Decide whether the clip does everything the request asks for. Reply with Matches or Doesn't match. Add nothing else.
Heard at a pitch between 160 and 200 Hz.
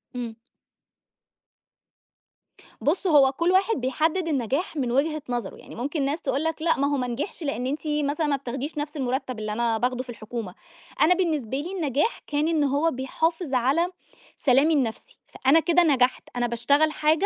Doesn't match